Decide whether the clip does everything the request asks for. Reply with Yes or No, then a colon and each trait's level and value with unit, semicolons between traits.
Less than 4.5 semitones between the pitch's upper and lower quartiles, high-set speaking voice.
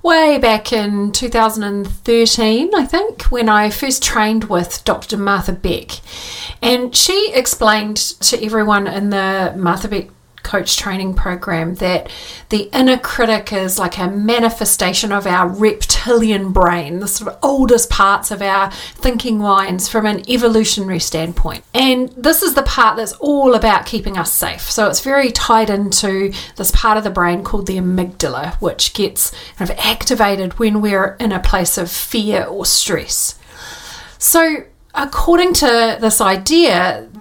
Yes: average, 3.8 semitones; high, 215 Hz